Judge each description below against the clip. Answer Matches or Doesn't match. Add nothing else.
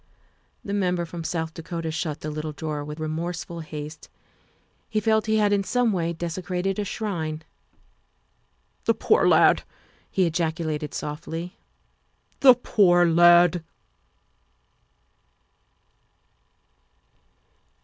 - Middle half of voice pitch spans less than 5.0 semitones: Matches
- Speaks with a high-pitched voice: Doesn't match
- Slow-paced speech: Matches